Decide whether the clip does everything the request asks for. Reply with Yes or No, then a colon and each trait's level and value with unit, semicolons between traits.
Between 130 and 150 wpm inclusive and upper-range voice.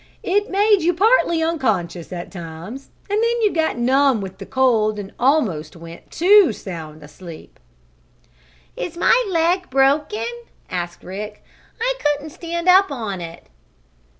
Yes: average, 140 wpm; very high, 265 Hz